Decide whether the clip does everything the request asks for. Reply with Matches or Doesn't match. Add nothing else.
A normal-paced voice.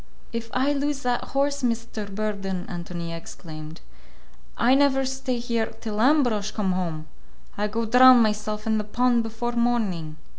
Matches